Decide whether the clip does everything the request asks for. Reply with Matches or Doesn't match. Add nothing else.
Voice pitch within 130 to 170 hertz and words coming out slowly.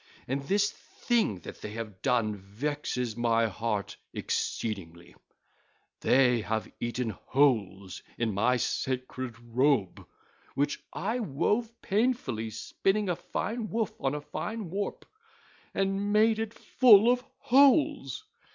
Matches